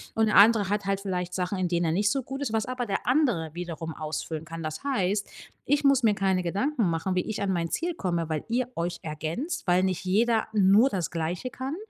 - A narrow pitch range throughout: No, wide, 5.4 semitones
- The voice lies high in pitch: Yes, high, 195 Hz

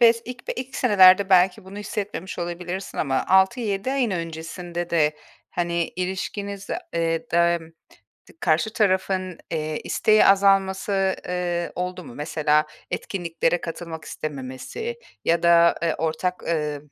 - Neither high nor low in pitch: Yes, medium, 180 Hz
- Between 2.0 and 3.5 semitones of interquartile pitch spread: Yes, average, 2.9 semitones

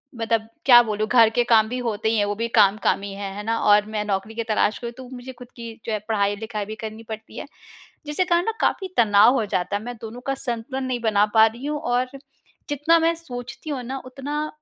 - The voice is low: No, high, 230 Hz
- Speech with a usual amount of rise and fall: Yes, average, 3.1 semitones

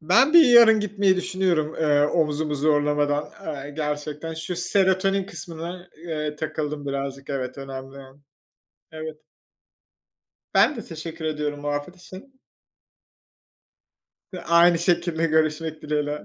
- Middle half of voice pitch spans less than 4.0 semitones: Yes, average, 3.1 semitones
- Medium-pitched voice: Yes, medium, 155 Hz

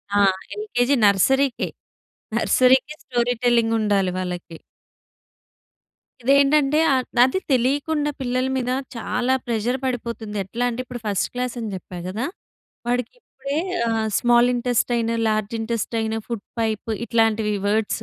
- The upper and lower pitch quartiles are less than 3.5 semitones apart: Yes, narrow, 2.6 semitones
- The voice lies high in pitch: Yes, high, 240 Hz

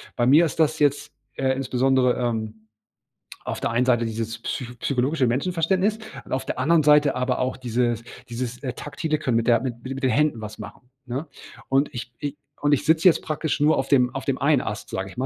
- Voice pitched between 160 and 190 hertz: No, low, 130 Hz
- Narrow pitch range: No, average, 3.5 semitones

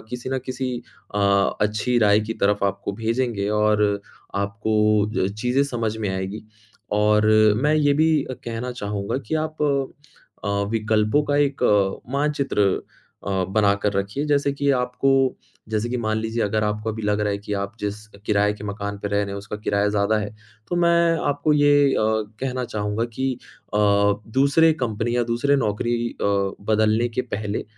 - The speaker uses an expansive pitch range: No, average, 3.9 semitones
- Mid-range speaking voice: No, low, 110 Hz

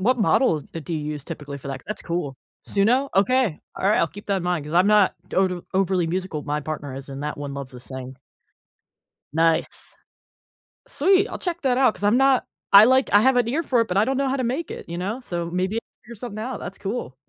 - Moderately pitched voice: No, high, 195 Hz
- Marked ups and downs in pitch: Yes, wide, 7.9 semitones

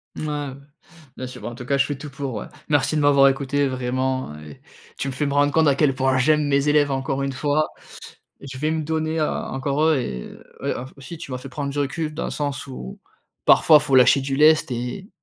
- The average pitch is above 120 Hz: Yes, medium, 140 Hz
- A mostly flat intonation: Yes, narrow, 2.2 semitones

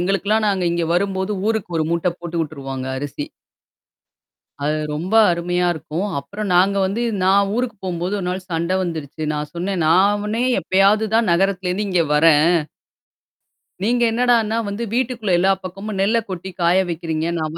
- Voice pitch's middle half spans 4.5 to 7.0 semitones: No, average, 3.4 semitones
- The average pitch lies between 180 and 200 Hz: Yes, medium, 185 Hz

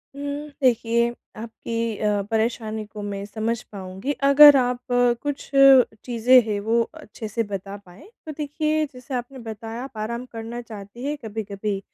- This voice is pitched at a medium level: No, high, 230 Hz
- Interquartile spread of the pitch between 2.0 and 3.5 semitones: Yes, average, 2.8 semitones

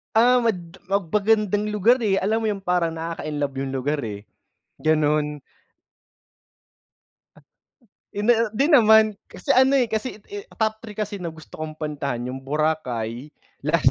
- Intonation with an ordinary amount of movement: No, wide, 6.3 semitones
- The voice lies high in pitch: No, medium, 180 Hz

